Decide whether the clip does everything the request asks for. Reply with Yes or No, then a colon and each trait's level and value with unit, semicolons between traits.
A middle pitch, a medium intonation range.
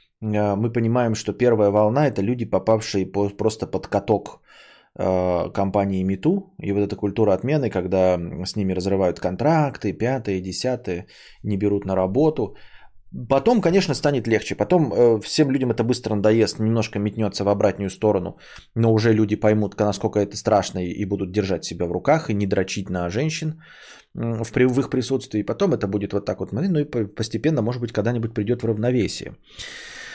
No: low, 110 Hz; average, 3.6 semitones